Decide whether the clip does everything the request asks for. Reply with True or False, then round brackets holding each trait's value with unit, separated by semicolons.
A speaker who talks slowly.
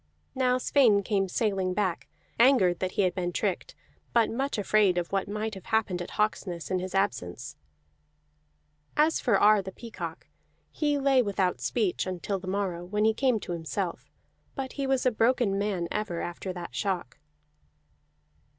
False (165 wpm)